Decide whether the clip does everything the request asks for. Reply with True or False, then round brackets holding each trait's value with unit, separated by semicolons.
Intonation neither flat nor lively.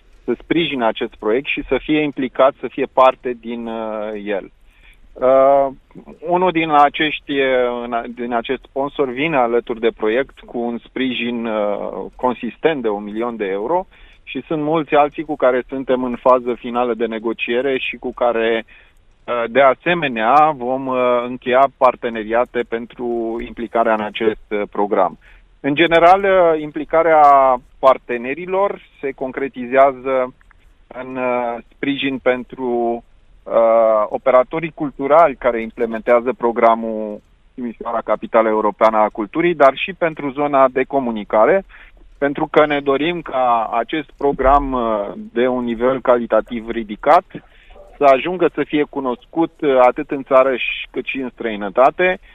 True (3.1 semitones)